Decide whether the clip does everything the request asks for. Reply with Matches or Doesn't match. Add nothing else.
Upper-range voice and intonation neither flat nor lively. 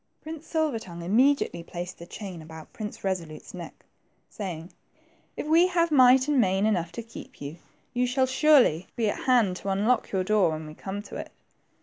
Doesn't match